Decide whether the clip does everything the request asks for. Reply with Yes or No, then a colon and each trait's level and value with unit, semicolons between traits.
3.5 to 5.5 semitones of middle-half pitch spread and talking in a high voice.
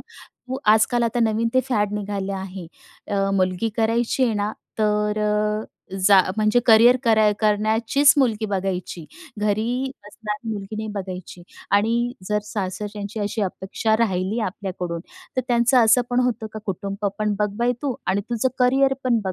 No: average, 2.8 semitones; high, 215 Hz